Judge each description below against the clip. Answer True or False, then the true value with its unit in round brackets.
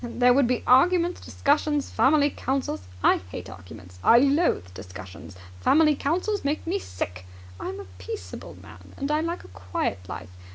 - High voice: True (250 Hz)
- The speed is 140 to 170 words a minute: True (160 wpm)